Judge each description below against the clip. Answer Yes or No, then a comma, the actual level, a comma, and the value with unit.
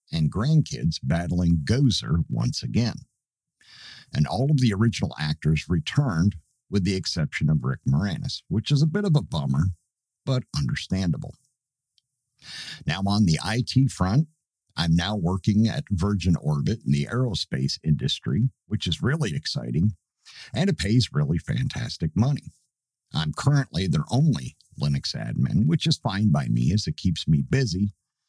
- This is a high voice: No, low, 110 Hz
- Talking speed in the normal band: Yes, average, 145 wpm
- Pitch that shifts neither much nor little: No, wide, 7.7 semitones